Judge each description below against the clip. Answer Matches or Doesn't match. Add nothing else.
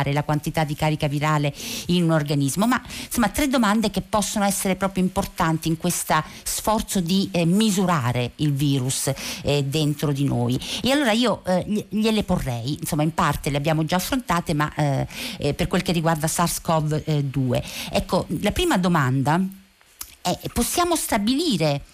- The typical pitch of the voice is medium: Matches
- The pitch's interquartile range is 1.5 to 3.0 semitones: Doesn't match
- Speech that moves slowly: Doesn't match